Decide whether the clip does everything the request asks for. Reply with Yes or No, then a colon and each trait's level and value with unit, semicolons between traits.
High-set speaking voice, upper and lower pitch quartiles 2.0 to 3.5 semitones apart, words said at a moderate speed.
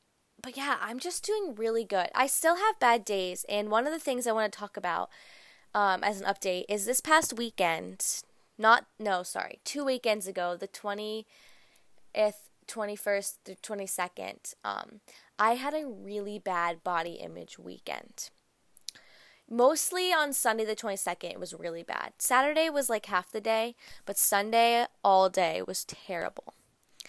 No: high, 215 Hz; average, 4.7 semitones; average, 155 wpm